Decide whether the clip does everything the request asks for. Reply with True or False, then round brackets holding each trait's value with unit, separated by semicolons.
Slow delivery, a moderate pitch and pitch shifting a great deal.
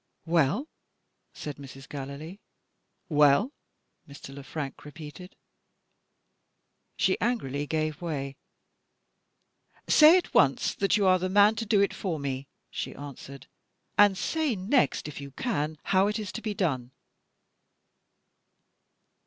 True (125 wpm; 160 Hz; 6.3 semitones)